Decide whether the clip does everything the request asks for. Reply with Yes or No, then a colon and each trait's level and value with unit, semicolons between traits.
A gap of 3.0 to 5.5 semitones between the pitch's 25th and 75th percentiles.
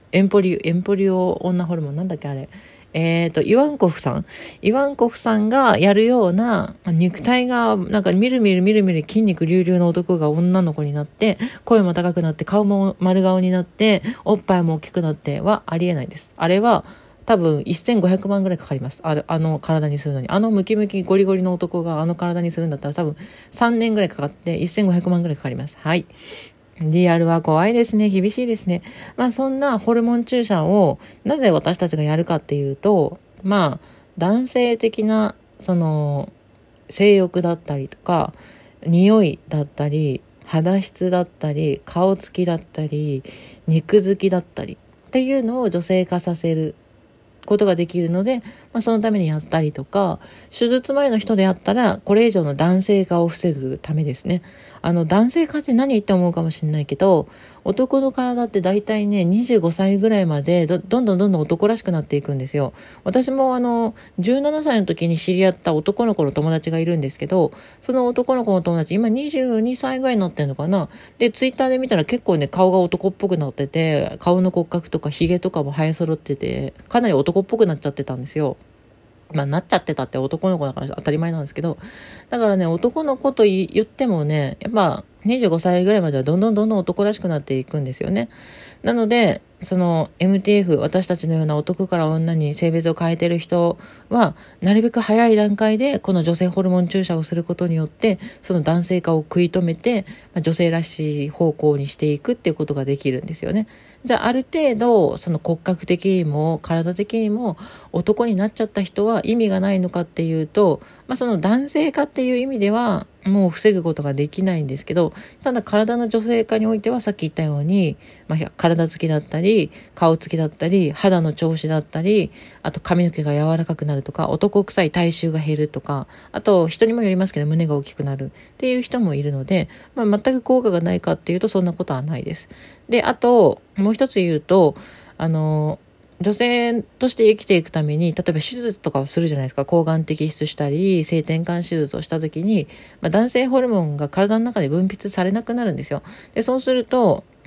Yes: average, 5.1 semitones